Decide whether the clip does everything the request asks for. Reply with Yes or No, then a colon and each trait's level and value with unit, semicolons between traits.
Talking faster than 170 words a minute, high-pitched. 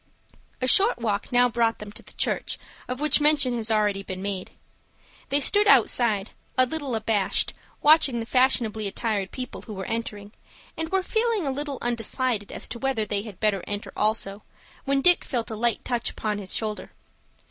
Yes: average, 180 wpm; high, 230 Hz